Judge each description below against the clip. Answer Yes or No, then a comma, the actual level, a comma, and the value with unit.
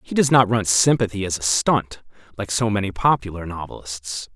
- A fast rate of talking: No, average, 180 wpm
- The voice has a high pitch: No, low, 100 Hz